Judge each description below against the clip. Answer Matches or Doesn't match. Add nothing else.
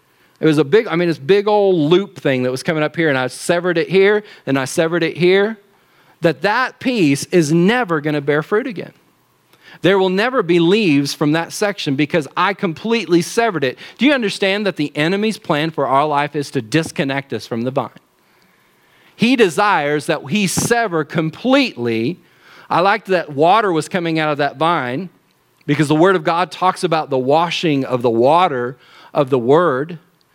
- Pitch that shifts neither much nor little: Matches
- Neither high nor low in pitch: Matches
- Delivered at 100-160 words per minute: Doesn't match